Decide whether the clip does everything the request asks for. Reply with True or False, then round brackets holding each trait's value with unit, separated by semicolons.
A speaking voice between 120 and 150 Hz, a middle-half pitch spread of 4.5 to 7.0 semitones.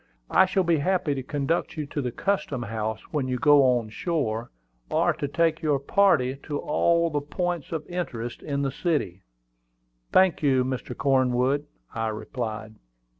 True (140 Hz; 4.8 semitones)